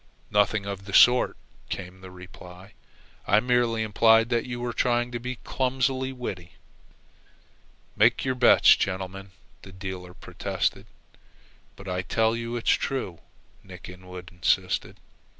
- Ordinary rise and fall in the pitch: Yes, average, 4.7 semitones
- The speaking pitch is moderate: No, low, 105 Hz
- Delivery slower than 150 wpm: Yes, slow, 135 wpm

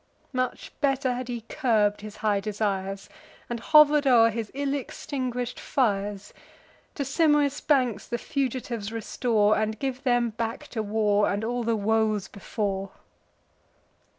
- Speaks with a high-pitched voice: Yes, high, 230 Hz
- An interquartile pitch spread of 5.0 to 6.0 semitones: No, average, 3.6 semitones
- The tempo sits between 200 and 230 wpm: No, slow, 135 wpm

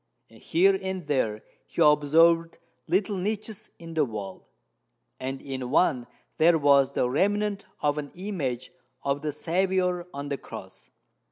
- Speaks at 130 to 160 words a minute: Yes, average, 140 wpm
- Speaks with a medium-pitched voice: Yes, medium, 155 Hz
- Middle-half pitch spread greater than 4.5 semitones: Yes, average, 5.2 semitones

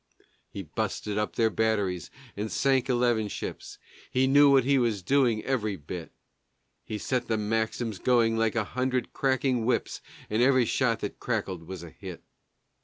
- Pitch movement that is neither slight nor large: Yes, average, 3.4 semitones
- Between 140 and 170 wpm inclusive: Yes, average, 165 wpm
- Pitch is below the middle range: Yes, low, 115 Hz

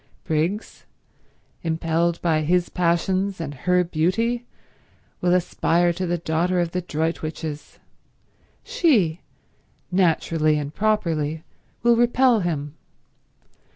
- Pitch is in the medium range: Yes, medium, 170 Hz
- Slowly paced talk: Yes, slow, 100 wpm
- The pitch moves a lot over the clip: No, average, 2.8 semitones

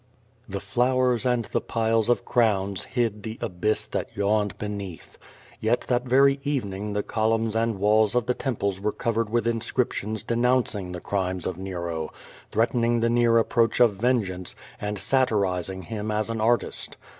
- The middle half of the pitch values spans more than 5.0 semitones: No, average, 3.0 semitones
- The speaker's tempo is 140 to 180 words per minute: Yes, average, 165 wpm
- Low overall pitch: Yes, low, 110 Hz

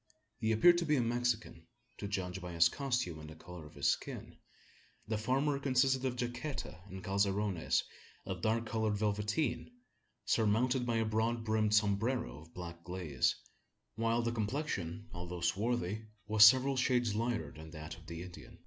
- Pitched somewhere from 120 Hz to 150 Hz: No, low, 110 Hz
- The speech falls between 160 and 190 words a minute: Yes, average, 165 wpm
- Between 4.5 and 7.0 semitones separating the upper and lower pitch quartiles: Yes, average, 5.2 semitones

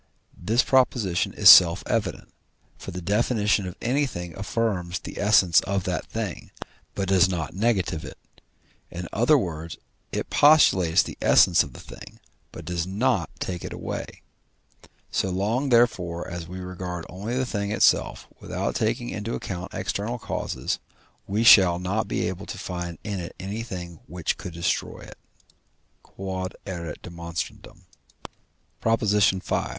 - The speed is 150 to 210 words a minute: No, average, 140 wpm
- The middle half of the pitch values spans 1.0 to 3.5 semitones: No, average, 4.0 semitones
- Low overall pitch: Yes, very low, 95 Hz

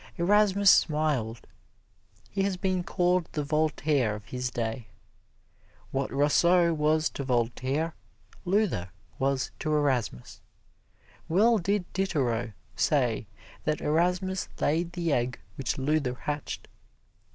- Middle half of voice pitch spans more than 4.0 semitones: Yes, wide, 5.6 semitones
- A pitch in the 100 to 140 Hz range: No, medium, 150 Hz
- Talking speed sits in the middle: No, slow, 110 wpm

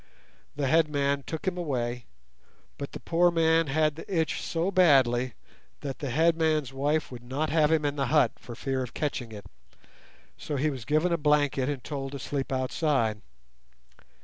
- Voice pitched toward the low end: No, medium, 145 Hz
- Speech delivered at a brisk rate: No, average, 175 wpm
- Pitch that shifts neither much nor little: Yes, average, 3.2 semitones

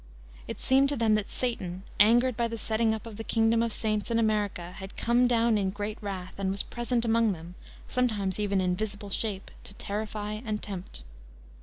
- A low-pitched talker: No, high, 215 Hz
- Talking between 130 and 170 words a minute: No, average, 200 wpm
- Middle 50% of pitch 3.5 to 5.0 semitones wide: No, narrow, 2.6 semitones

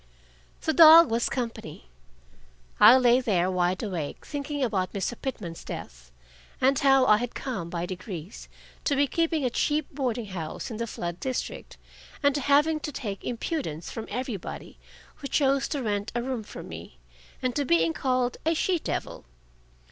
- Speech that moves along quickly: No, average, 165 wpm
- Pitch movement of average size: No, wide, 6.9 semitones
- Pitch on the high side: Yes, high, 245 Hz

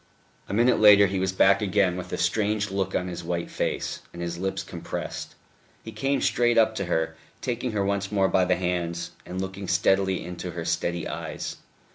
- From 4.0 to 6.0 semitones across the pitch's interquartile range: No, average, 2.7 semitones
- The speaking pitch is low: Yes, very low, 95 Hz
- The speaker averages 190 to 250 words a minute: Yes, average, 195 wpm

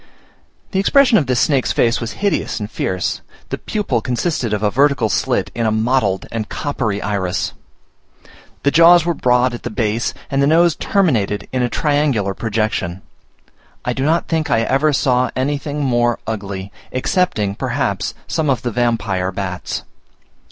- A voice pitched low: Yes, low, 125 Hz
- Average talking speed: Yes, average, 160 wpm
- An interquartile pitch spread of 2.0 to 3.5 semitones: No, wide, 5.4 semitones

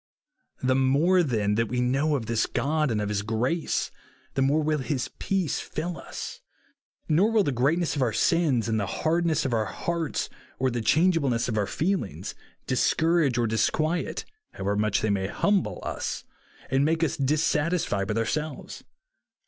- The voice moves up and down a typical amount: No, wide, 6.0 semitones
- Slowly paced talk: No, average, 170 wpm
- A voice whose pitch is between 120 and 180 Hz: Yes, low, 135 Hz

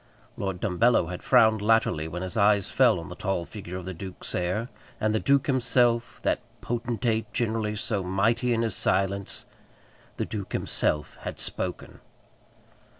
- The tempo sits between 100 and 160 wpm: Yes, average, 155 wpm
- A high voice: No, low, 105 Hz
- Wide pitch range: No, average, 3.8 semitones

